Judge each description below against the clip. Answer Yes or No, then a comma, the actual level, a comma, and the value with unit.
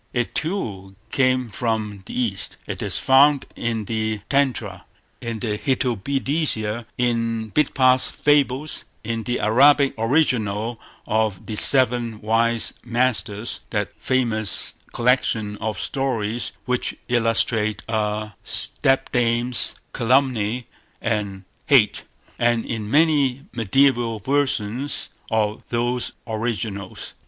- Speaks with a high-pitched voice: No, low, 115 Hz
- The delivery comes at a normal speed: No, slow, 105 wpm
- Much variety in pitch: No, average, 3.0 semitones